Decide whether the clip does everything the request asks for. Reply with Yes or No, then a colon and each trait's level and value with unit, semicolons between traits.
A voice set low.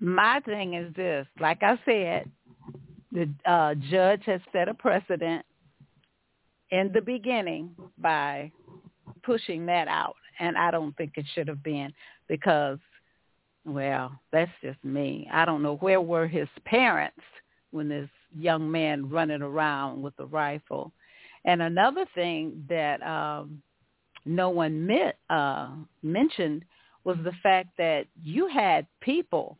No: medium, 165 Hz